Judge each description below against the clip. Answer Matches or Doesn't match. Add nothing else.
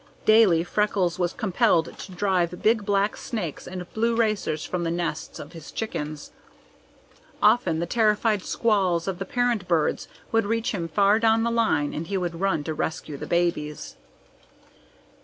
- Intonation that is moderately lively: Matches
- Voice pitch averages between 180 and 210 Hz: Matches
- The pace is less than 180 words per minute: Matches